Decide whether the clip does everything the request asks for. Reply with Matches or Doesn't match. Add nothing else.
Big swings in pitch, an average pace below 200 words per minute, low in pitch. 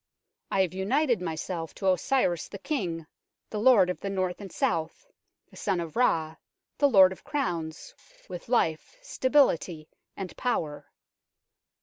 Doesn't match